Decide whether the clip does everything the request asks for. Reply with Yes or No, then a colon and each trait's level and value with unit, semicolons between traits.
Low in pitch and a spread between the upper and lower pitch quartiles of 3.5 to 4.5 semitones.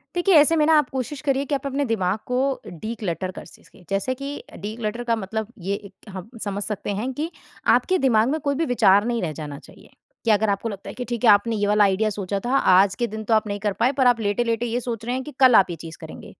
No: high, 225 Hz; average, 4.1 semitones